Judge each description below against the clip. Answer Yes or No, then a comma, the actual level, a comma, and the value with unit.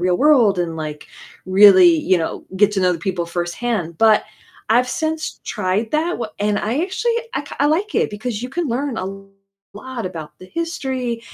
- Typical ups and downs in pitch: No, wide, 6.8 semitones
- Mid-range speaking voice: No, high, 220 Hz